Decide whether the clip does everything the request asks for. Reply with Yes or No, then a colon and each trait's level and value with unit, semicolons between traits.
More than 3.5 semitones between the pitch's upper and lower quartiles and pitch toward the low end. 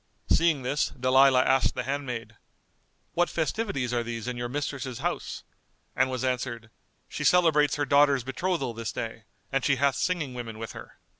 No: average, 3.0 semitones; low, 130 Hz